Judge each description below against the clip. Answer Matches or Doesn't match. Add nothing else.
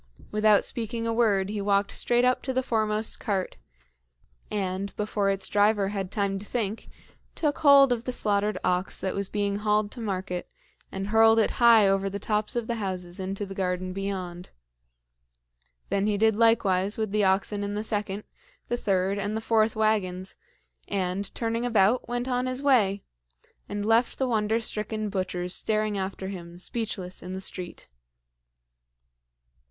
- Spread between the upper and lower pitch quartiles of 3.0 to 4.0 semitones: Doesn't match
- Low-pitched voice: Doesn't match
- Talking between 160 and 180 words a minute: Matches